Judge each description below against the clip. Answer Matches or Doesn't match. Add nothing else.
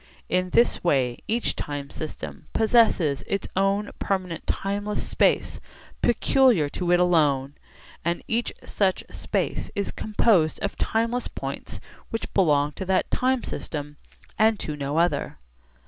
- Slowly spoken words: Matches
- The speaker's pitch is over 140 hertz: Matches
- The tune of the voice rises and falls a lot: Matches